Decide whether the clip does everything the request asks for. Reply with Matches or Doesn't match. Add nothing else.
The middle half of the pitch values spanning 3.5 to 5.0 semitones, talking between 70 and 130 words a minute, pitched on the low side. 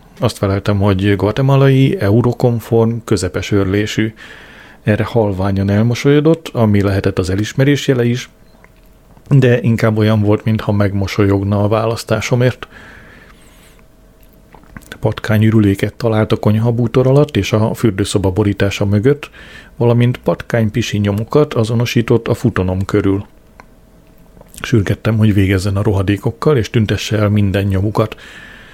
Doesn't match